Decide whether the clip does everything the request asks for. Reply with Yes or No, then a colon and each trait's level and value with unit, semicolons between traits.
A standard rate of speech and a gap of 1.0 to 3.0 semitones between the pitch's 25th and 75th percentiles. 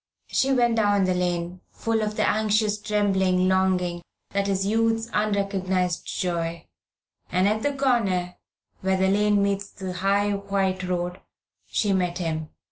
Yes: average, 145 wpm; narrow, 2.4 semitones